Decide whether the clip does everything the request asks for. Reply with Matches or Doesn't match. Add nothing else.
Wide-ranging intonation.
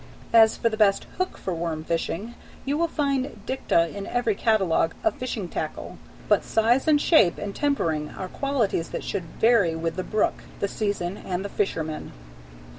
Matches